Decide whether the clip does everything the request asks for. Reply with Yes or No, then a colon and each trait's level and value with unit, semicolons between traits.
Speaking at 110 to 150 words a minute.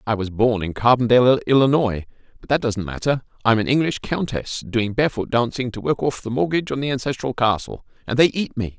No: average, 200 wpm